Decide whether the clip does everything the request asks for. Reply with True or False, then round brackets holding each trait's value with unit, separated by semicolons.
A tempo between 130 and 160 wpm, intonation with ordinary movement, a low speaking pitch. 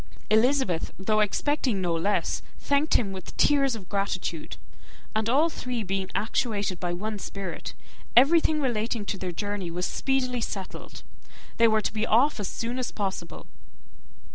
False (150 wpm; 4.5 semitones; 215 Hz)